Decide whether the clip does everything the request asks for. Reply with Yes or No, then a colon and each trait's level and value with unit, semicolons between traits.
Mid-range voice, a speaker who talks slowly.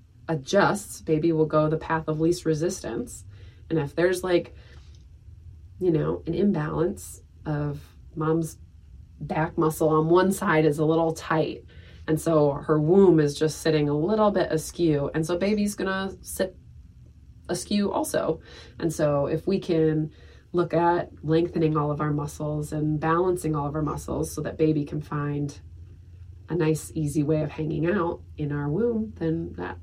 No: medium, 155 Hz; average, 165 wpm